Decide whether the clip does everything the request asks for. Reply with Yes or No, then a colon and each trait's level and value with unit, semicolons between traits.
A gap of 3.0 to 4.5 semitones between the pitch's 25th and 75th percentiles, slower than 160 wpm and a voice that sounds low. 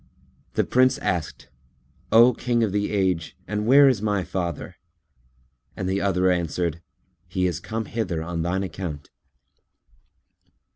Yes: average, 3.8 semitones; slow, 135 wpm; very low, 95 Hz